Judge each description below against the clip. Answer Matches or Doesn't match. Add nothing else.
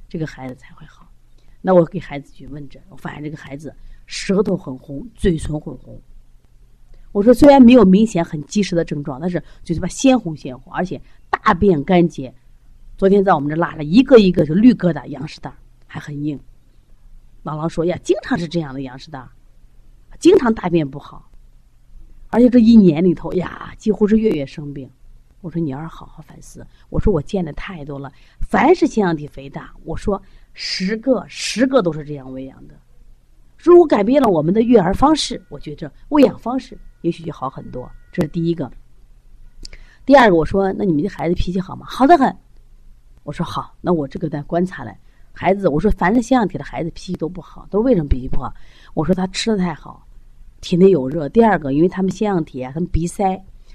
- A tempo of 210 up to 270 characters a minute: Doesn't match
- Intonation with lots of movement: Matches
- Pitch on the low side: Doesn't match